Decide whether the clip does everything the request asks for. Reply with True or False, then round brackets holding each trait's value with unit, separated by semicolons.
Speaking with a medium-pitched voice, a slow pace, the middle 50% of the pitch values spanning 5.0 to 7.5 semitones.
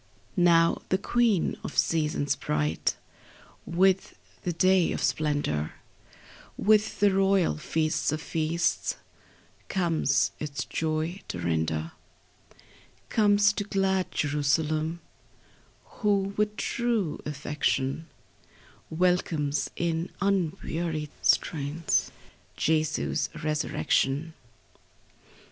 False (165 Hz; 85 wpm; 4.2 semitones)